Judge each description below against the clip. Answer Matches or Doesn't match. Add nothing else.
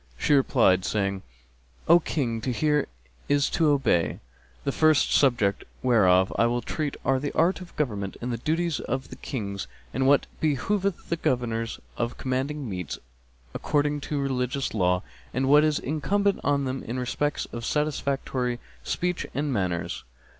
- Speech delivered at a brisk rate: Doesn't match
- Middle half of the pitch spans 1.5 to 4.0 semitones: Doesn't match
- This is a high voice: Doesn't match